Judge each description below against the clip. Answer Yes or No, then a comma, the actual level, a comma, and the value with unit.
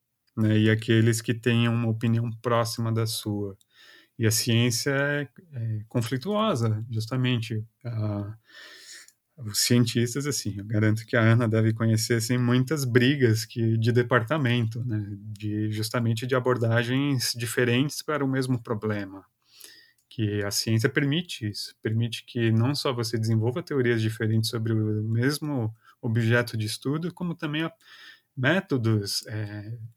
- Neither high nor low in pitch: No, low, 115 Hz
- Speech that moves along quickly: No, average, 135 wpm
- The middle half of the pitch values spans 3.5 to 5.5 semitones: No, narrow, 2.4 semitones